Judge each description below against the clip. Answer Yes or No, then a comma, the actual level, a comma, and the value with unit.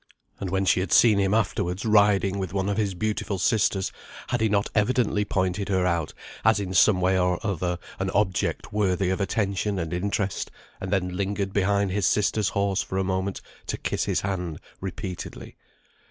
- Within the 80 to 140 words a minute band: No, average, 185 wpm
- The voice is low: Yes, very low, 95 Hz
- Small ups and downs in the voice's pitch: Yes, narrow, 1.7 semitones